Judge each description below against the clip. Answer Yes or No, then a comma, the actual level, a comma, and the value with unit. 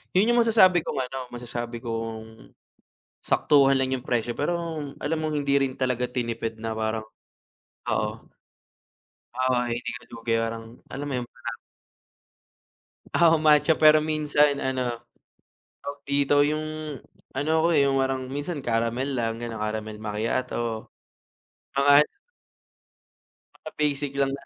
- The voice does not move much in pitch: No, average, 4.1 semitones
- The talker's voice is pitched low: Yes, low, 130 Hz